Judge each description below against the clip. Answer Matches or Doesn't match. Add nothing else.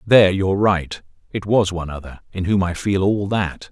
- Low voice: Matches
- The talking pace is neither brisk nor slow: Doesn't match